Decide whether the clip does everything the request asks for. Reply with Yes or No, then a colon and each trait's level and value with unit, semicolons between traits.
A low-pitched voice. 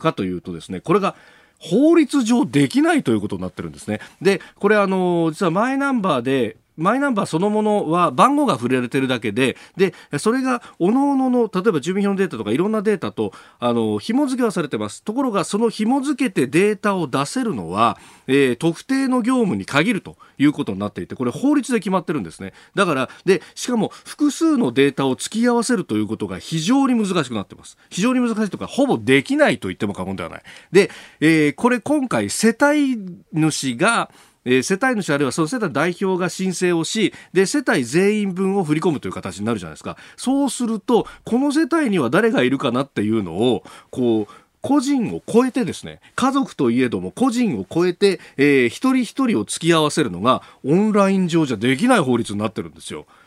No: high, 190 Hz